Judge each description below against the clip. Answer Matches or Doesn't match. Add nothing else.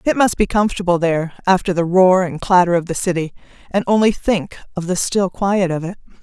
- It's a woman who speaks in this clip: Matches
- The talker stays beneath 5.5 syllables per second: Doesn't match